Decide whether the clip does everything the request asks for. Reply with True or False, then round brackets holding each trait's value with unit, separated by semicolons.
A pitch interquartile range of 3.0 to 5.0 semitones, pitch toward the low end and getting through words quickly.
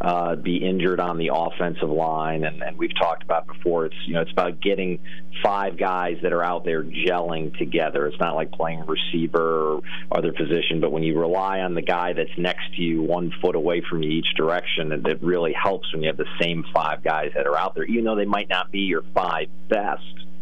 False (2.4 semitones; 85 Hz; 225 wpm)